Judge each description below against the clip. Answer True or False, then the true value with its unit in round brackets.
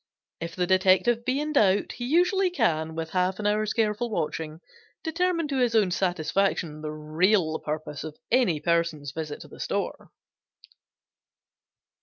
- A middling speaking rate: True (150 wpm)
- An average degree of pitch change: False (7.1 semitones)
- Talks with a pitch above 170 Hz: True (185 Hz)